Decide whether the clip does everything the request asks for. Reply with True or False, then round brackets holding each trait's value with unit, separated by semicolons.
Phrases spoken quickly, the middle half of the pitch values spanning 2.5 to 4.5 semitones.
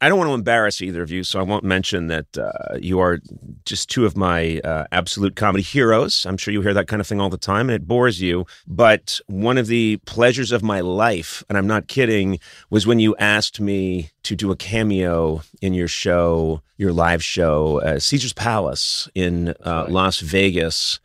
True (210 wpm; 3.5 semitones)